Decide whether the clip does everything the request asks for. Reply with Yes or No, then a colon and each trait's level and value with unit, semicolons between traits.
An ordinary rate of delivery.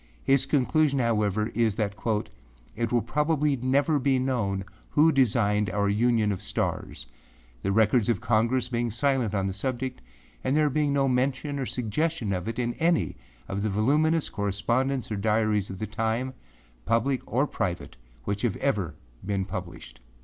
Yes: average, 160 wpm